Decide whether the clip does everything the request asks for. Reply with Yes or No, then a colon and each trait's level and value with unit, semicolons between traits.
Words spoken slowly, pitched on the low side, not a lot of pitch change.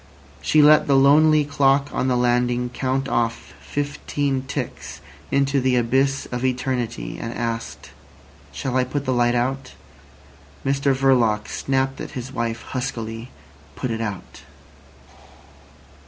Yes: slow, 130 wpm; low, 130 Hz; narrow, 2.3 semitones